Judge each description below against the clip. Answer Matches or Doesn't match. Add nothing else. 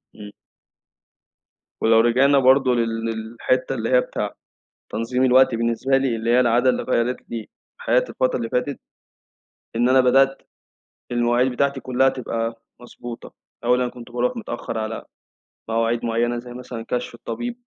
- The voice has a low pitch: Matches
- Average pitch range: Doesn't match